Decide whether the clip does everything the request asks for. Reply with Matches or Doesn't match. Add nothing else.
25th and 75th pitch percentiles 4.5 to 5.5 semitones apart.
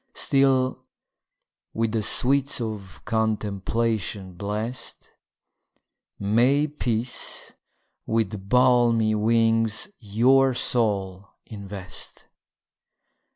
Doesn't match